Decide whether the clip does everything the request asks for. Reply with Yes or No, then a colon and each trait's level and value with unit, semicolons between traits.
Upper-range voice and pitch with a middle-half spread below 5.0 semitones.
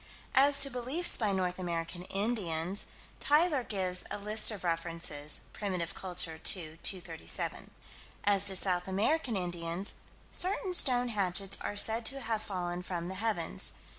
Yes: high, 195 Hz; average, 4.3 semitones